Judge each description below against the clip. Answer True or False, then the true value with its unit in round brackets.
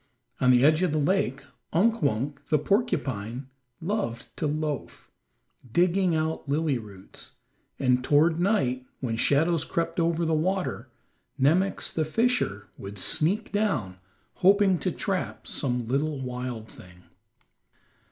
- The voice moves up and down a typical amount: False (6.0 semitones)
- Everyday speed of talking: False (130 wpm)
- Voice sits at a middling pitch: True (150 Hz)